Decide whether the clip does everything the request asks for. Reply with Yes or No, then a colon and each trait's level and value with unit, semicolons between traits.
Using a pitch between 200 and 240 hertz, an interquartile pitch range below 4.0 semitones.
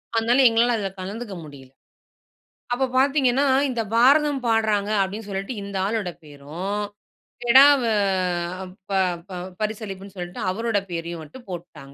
No: high, 210 Hz; average, 4.3 semitones